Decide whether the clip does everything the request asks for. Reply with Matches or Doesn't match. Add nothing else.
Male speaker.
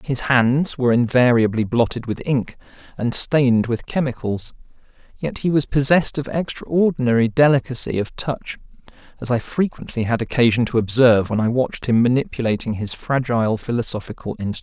Matches